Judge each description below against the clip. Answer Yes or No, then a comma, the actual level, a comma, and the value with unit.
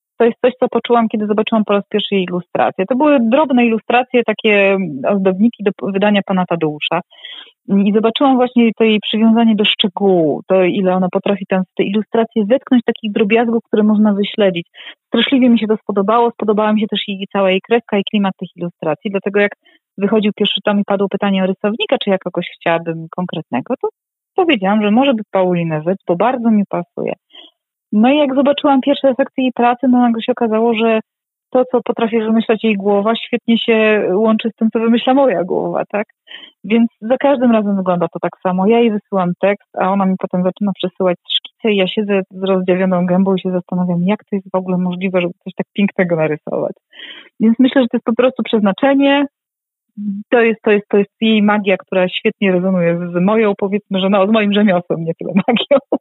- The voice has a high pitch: Yes, high, 210 Hz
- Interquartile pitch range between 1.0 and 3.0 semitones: No, average, 3.6 semitones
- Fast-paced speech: Yes, fast, 200 wpm